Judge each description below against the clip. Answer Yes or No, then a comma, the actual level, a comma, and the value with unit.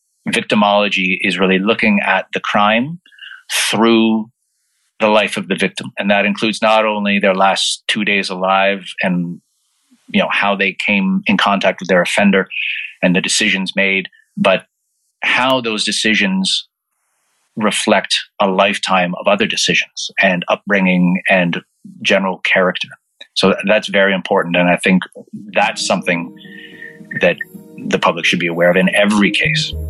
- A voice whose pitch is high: No, low, 100 Hz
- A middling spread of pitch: No, narrow, 2.3 semitones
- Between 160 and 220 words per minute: No, average, 145 wpm